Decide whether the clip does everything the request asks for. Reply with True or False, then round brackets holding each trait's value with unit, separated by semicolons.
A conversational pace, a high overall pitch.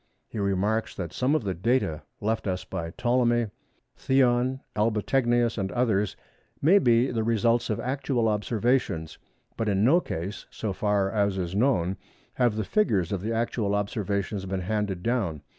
False (160 wpm; 110 Hz)